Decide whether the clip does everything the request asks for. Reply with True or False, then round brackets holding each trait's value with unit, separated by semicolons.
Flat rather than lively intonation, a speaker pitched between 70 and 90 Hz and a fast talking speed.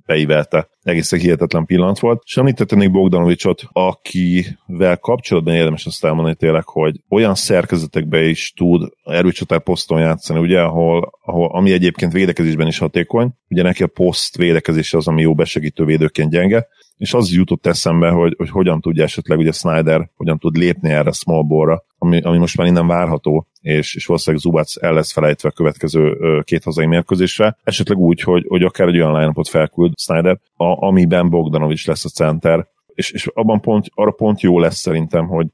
True (2.2 semitones; 85 Hz; 170 wpm)